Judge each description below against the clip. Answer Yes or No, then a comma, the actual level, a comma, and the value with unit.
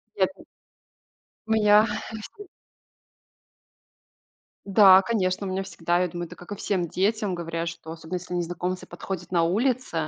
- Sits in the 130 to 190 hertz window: Yes, medium, 185 Hz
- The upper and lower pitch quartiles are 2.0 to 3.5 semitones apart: Yes, average, 3.1 semitones